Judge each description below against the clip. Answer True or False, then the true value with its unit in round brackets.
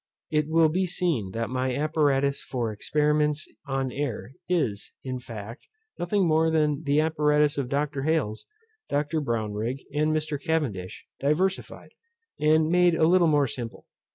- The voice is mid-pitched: True (150 Hz)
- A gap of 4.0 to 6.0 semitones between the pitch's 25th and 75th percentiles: False (3.6 semitones)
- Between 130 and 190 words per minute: True (145 wpm)